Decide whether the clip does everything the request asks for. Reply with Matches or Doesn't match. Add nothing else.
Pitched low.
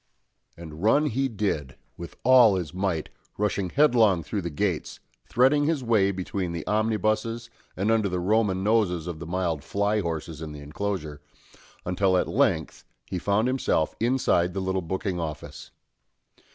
Matches